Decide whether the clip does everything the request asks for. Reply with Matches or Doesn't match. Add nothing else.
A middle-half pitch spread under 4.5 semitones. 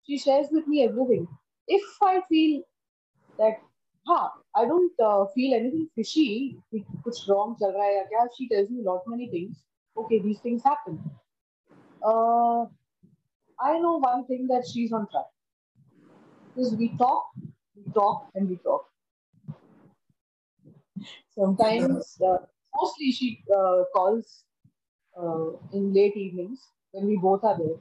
Doesn't match